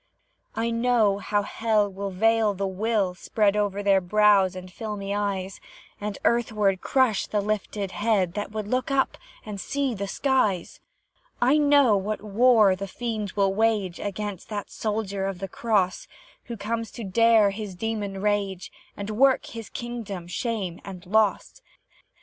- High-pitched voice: Yes, high, 210 Hz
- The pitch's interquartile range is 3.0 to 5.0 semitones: No, narrow, 2.5 semitones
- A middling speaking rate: Yes, average, 150 wpm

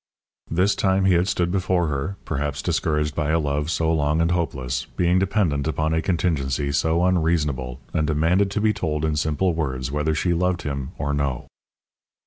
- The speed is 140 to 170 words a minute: No, average, 180 wpm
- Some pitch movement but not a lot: Yes, average, 3.4 semitones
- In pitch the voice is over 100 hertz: No, very low, 80 Hz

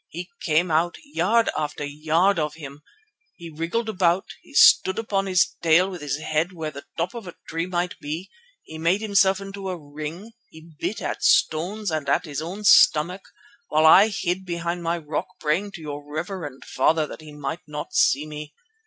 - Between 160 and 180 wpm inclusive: No, average, 190 wpm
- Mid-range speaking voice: Yes, medium, 170 Hz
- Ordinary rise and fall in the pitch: Yes, average, 3.6 semitones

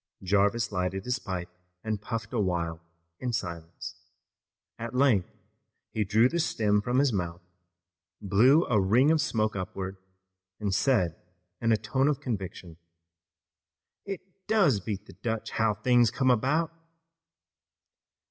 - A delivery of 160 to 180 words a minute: No, slow, 135 wpm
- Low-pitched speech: Yes, low, 110 Hz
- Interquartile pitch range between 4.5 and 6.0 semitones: Yes, average, 4.8 semitones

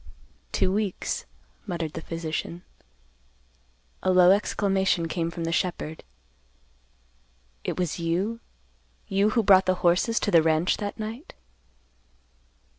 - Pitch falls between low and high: Yes, medium, 180 Hz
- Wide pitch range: No, average, 3.2 semitones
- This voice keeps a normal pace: No, slow, 115 wpm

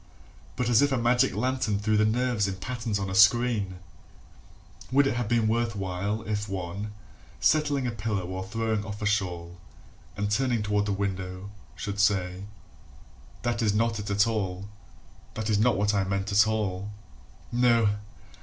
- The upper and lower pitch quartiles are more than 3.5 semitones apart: No, average, 2.9 semitones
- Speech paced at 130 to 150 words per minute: No, average, 170 wpm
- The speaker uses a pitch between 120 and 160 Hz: No, low, 105 Hz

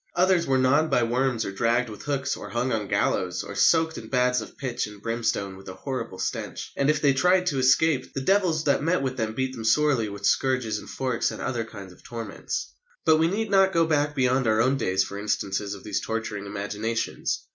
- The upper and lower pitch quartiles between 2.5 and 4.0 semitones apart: No, average, 5.2 semitones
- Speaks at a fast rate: Yes, fast, 220 wpm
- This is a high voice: No, low, 125 Hz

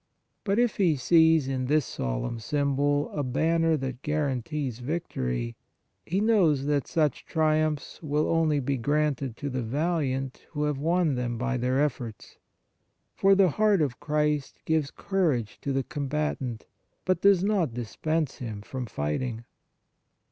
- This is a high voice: No, medium, 145 Hz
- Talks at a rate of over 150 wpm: No, average, 145 wpm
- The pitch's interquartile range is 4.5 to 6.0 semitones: No, average, 4.0 semitones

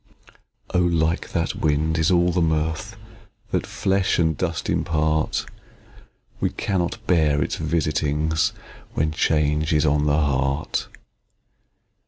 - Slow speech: Yes, slow, 120 wpm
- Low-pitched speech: Yes, very low, 80 Hz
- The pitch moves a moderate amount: No, narrow, 1.8 semitones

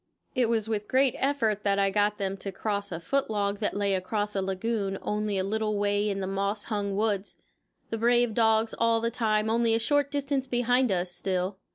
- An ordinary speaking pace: No, fast, 210 wpm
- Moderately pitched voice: No, high, 210 Hz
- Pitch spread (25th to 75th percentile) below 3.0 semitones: Yes, narrow, 2.6 semitones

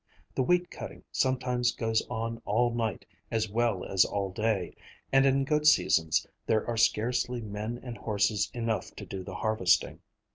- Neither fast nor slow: Yes, average, 160 wpm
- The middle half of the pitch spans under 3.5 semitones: Yes, average, 2.9 semitones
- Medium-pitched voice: No, low, 115 Hz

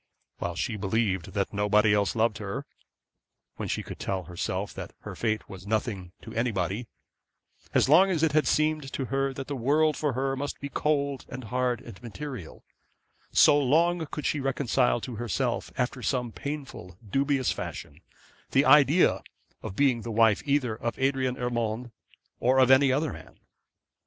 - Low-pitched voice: Yes, low, 125 Hz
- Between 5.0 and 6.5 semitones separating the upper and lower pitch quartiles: No, average, 4.5 semitones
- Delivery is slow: No, average, 165 wpm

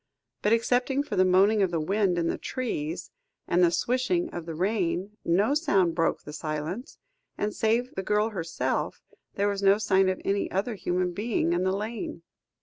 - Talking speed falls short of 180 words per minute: No, average, 185 wpm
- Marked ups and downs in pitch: No, average, 3.8 semitones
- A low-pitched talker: No, high, 195 Hz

